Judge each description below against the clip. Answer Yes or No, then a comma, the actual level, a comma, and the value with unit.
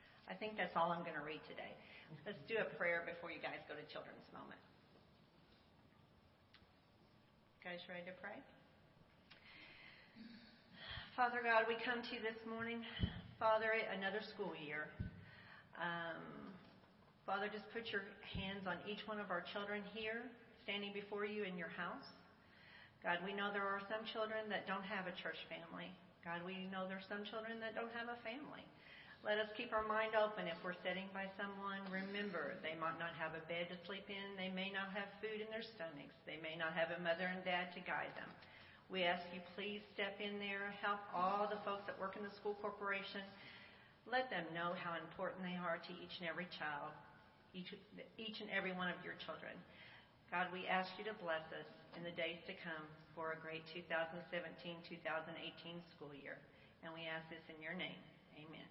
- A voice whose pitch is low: No, high, 190 Hz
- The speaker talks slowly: No, average, 185 wpm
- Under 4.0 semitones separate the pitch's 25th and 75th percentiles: Yes, average, 3.6 semitones